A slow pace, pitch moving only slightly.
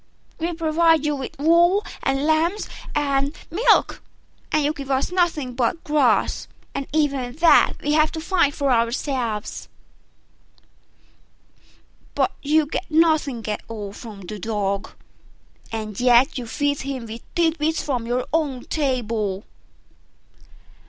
No: slow, 130 wpm; average, 4.9 semitones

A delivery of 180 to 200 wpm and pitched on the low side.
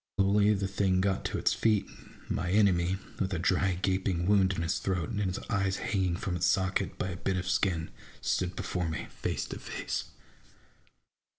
Yes: average, 190 wpm; very low, 95 Hz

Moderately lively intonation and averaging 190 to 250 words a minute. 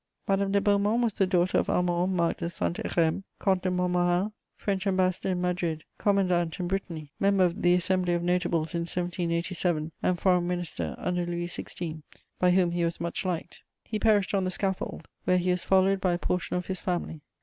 No: narrow, 1.6 semitones; average, 195 wpm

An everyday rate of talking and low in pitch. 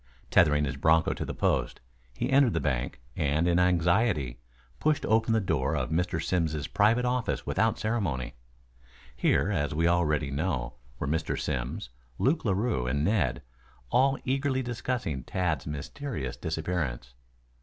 Yes: average, 145 wpm; very low, 85 Hz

